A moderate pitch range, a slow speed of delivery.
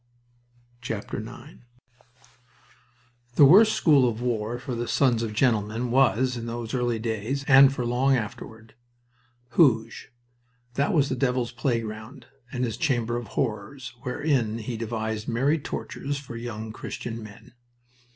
Yes: average, 3.2 semitones; slow, 130 wpm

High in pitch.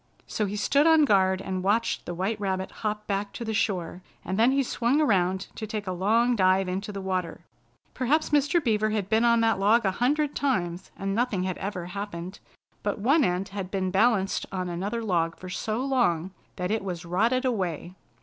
Yes: high, 200 Hz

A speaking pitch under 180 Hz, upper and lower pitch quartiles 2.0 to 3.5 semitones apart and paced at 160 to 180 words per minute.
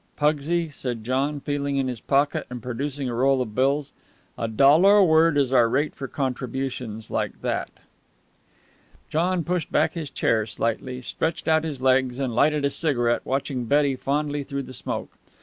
Yes: low, 135 Hz; average, 2.8 semitones; average, 170 wpm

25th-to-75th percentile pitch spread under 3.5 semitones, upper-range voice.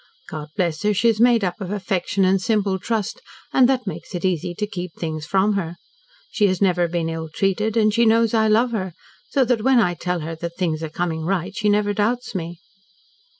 No: average, 3.9 semitones; high, 195 Hz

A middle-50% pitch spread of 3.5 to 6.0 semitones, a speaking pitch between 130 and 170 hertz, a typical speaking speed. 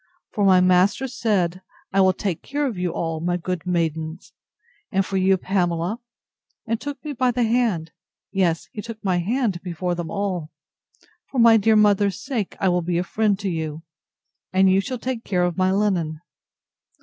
No: average, 3.9 semitones; high, 190 Hz; average, 185 wpm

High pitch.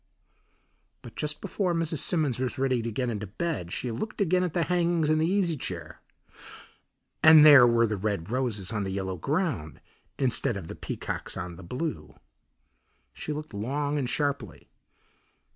No: low, 130 Hz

